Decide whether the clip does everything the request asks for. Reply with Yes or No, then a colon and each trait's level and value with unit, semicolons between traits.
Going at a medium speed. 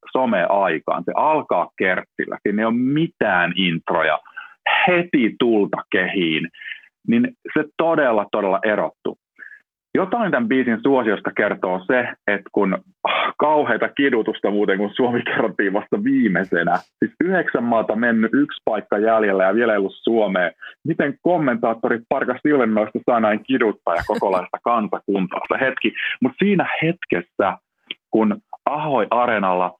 Yes: average, 125 wpm